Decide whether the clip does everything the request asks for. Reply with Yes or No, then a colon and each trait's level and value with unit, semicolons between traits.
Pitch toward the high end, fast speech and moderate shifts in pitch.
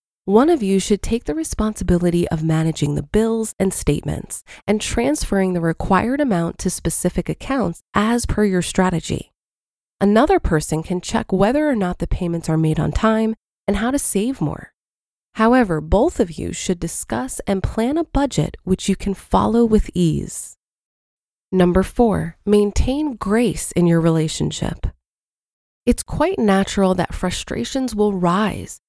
No: high, 195 Hz; average, 150 wpm; average, 4.4 semitones